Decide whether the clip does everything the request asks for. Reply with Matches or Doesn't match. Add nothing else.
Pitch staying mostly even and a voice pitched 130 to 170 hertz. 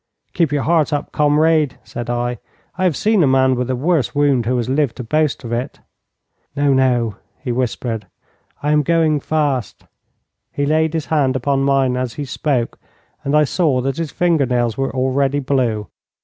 Doesn't match